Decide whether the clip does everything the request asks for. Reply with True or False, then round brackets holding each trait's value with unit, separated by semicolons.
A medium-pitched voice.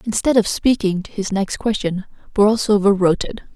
False (205 Hz)